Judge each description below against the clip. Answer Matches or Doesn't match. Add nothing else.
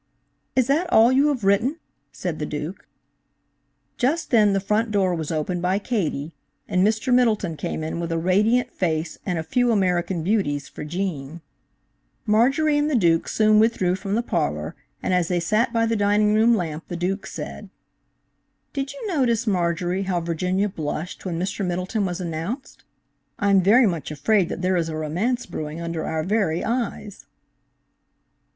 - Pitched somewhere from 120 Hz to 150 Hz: Doesn't match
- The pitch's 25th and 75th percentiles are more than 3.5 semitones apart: Matches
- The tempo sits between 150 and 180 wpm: Matches